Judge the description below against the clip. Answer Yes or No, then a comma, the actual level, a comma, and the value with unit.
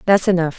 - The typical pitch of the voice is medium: Yes, medium, 180 Hz